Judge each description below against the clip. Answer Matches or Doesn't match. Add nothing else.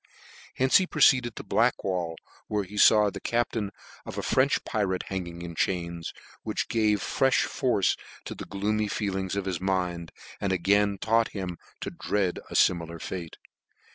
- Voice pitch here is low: Matches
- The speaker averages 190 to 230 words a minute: Doesn't match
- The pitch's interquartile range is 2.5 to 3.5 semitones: Matches